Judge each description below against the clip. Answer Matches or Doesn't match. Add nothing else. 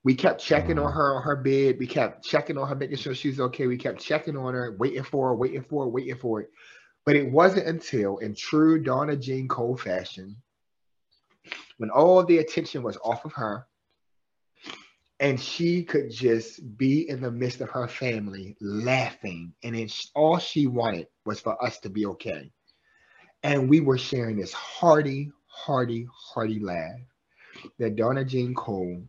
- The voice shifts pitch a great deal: Doesn't match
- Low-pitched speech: Matches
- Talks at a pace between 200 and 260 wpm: Doesn't match